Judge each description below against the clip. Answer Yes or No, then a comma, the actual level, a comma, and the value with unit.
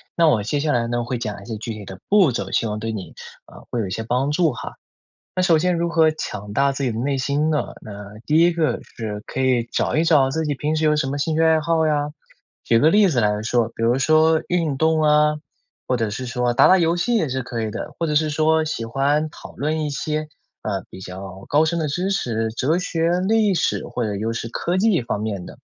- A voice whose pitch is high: No, medium, 140 Hz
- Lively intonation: Yes, wide, 5.7 semitones